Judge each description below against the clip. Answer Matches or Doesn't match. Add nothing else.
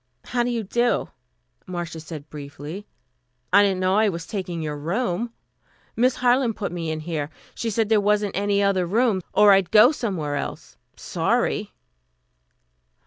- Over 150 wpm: Matches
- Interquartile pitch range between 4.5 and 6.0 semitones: Matches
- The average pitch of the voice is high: Matches